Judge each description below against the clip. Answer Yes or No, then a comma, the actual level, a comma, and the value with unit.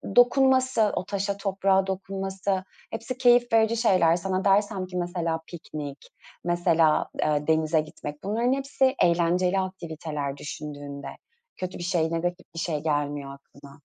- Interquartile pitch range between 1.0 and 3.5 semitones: No, average, 4.1 semitones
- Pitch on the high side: No, medium, 180 Hz